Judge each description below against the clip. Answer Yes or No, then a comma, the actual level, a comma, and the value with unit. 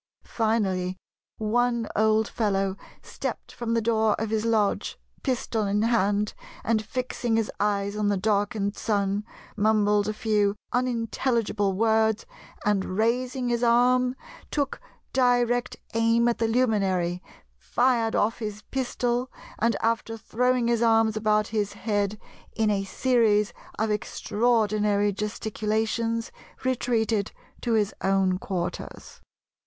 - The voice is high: Yes, high, 220 Hz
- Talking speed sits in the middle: No, slow, 120 wpm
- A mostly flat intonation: Yes, narrow, 2.2 semitones